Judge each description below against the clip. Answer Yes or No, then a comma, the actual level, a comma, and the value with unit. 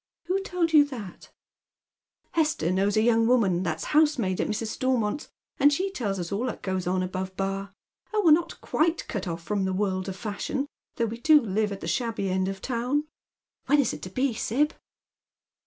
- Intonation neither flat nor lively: No, wide, 7.1 semitones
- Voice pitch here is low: No, high, 220 Hz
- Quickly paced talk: Yes, fast, 210 wpm